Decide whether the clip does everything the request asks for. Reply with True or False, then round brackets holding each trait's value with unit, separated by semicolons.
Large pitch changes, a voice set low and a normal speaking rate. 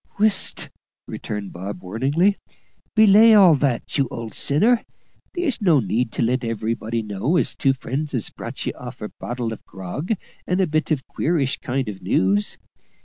True (7.8 semitones; 130 Hz; 165 wpm)